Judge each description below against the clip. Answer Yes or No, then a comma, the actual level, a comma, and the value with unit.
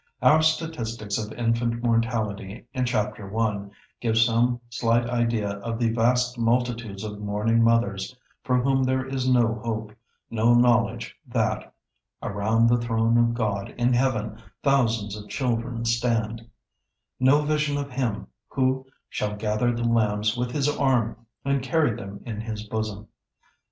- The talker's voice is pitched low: Yes, low, 115 Hz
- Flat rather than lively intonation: Yes, narrow, 2.3 semitones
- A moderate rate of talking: Yes, average, 145 wpm